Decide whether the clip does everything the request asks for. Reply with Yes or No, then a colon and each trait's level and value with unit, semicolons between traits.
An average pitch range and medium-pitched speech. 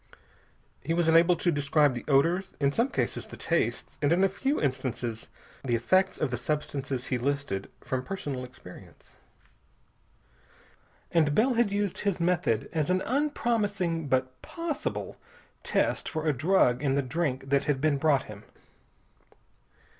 No: wide, 5.8 semitones; medium, 150 Hz